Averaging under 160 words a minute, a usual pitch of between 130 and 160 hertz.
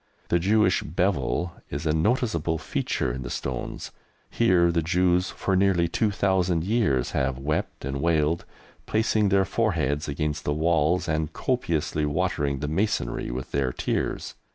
No: average, 150 wpm; very low, 85 Hz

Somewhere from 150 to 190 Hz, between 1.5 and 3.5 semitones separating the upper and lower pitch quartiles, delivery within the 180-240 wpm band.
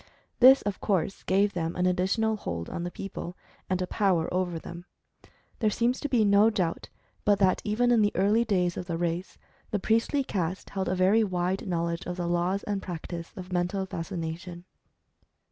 Yes: medium, 185 Hz; average, 2.9 semitones; average, 185 wpm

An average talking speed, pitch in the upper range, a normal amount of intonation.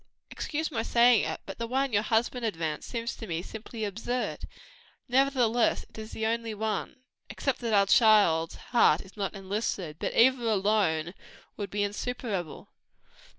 Yes: average, 155 wpm; high, 220 Hz; average, 3.3 semitones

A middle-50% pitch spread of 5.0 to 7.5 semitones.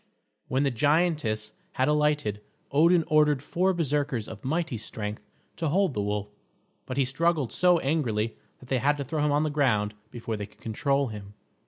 Yes: wide, 5.6 semitones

